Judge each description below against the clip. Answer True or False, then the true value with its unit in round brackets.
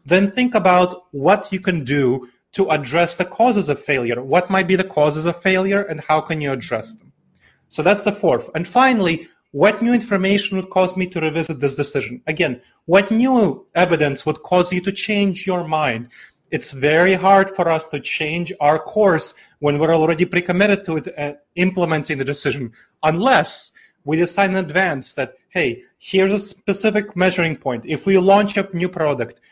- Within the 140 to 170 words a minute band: False (185 wpm)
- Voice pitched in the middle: True (175 Hz)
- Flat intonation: False (4.4 semitones)